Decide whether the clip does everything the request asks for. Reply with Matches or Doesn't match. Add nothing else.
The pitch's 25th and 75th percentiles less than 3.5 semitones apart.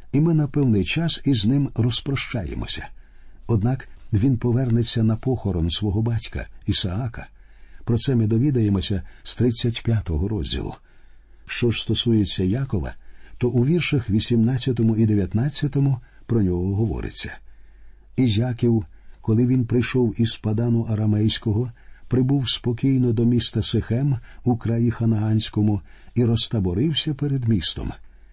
Matches